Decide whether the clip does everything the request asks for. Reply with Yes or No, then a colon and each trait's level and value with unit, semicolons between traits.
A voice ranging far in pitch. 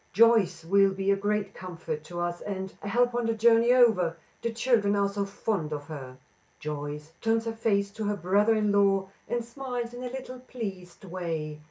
No: average, 4.3 semitones